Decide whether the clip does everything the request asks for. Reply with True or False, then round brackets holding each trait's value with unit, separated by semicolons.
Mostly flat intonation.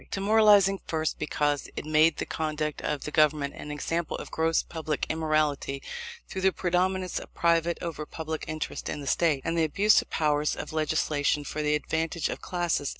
True (2.1 semitones)